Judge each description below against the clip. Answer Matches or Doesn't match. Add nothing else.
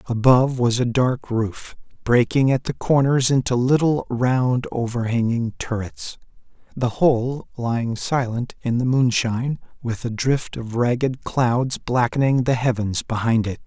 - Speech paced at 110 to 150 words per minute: Matches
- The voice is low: Matches